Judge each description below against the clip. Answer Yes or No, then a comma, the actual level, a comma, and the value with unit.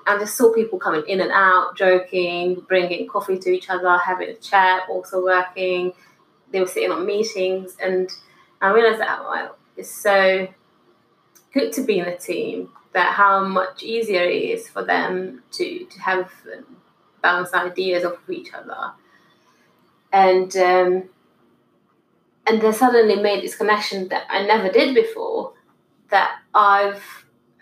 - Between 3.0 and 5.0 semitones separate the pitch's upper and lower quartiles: No, narrow, 2.4 semitones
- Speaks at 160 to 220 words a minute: No, average, 150 wpm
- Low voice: No, high, 190 Hz